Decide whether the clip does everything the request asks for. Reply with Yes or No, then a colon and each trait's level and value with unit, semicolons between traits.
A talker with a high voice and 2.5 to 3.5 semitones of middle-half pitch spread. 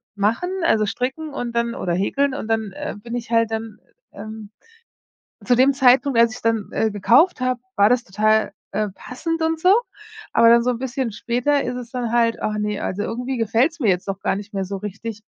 Yes: high, 230 Hz; average, 3.0 semitones